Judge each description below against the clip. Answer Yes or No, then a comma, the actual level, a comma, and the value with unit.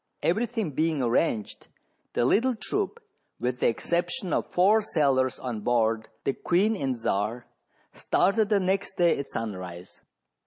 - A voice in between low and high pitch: Yes, medium, 155 Hz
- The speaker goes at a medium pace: Yes, average, 145 wpm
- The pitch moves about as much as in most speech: No, wide, 8.9 semitones